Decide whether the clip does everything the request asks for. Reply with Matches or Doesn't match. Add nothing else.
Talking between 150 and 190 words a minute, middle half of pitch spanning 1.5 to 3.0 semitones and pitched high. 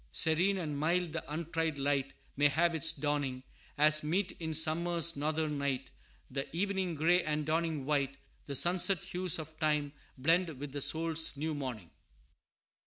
Doesn't match